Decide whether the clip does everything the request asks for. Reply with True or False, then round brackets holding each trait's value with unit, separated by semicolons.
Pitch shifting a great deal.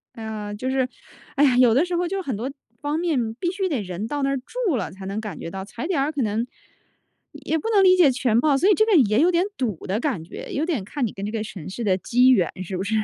True (7.0 semitones)